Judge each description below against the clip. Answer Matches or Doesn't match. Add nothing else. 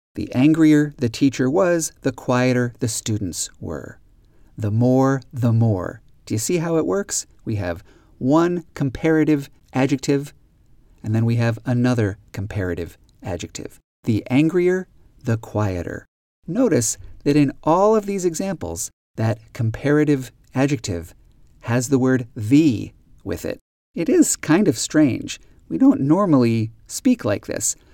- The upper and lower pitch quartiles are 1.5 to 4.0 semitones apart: Doesn't match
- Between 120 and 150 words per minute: Matches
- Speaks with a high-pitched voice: Doesn't match